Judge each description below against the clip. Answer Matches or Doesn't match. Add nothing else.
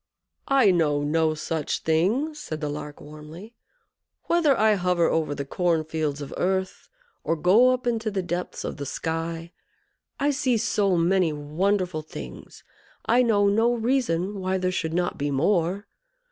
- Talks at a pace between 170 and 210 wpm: Doesn't match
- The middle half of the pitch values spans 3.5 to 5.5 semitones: Matches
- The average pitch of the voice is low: Doesn't match